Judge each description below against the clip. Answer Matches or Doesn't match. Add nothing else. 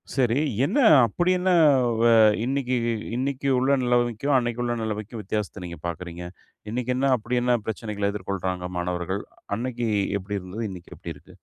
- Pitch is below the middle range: Matches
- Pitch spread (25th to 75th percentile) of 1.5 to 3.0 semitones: Doesn't match